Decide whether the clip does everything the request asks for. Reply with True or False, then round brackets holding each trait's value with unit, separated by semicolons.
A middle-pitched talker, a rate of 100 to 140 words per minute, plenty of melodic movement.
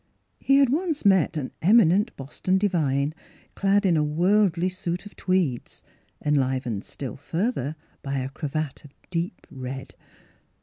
True (165 Hz; 135 wpm; 6.0 semitones)